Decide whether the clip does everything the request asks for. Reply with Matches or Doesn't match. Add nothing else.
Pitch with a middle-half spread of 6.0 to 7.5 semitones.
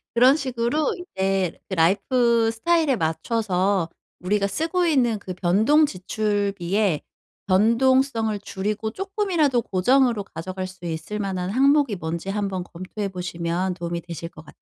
Doesn't match